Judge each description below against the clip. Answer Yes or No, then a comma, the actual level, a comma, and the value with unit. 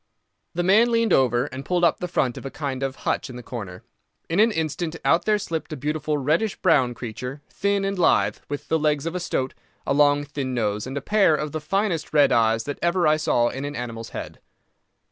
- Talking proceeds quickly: Yes, fast, 225 wpm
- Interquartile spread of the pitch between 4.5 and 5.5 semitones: Yes, average, 4.8 semitones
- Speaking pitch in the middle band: Yes, medium, 150 Hz